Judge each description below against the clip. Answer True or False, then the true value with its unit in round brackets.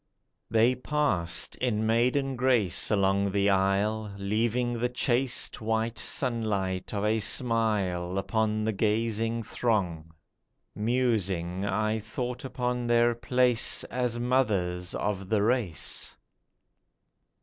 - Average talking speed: False (105 wpm)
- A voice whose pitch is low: True (110 Hz)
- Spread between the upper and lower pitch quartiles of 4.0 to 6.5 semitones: False (3.6 semitones)